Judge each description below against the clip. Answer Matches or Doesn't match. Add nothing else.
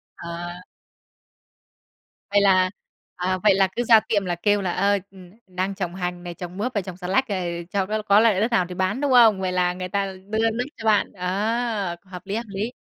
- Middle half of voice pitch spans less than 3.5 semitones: Matches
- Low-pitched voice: Doesn't match